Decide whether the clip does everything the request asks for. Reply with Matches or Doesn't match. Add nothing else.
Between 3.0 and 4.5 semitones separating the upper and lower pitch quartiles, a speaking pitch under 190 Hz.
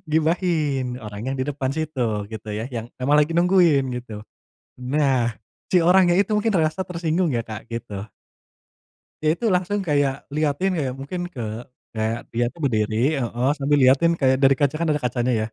Doesn't match